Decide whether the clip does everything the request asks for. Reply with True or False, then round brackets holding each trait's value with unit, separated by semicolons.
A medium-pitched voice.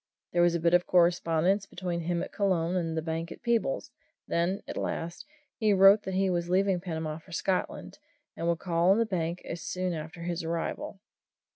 True (175 Hz)